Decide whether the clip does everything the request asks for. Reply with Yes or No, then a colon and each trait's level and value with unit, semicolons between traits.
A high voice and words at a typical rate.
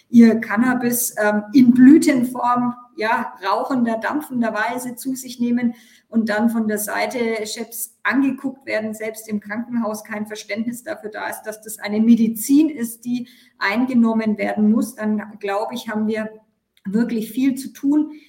Yes: high, 230 Hz; average, 150 wpm